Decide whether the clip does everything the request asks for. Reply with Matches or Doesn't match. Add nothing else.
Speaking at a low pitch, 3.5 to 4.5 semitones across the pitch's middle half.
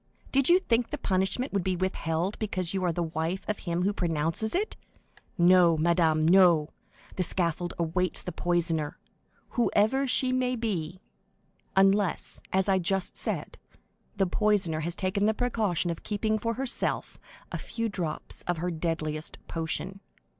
Doesn't match